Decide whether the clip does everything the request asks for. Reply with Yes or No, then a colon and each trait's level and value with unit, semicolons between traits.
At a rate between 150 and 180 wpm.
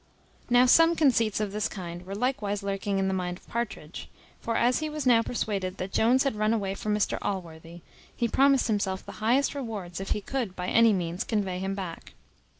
No: fast, 205 wpm